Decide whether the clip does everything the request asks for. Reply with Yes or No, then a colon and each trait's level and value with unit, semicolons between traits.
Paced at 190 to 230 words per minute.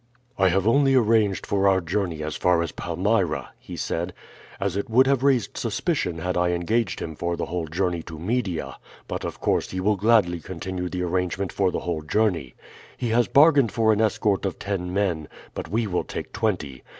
Yes: average, 200 wpm